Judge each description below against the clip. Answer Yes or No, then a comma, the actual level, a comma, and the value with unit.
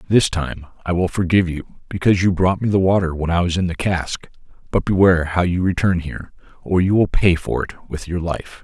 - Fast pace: Yes, fast, 230 wpm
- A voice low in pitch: Yes, very low, 90 Hz